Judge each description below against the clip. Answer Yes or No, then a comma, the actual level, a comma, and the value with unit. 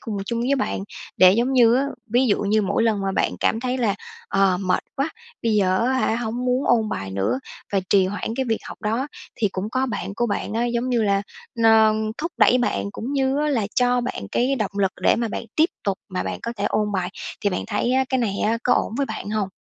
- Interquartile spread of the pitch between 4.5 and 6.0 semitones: No, average, 3.8 semitones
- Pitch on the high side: Yes, high, 225 Hz